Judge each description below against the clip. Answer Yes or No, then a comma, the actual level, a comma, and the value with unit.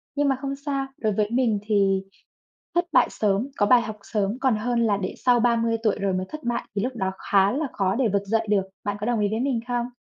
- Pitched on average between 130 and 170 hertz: No, high, 225 Hz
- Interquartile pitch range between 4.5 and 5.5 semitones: No, average, 3.5 semitones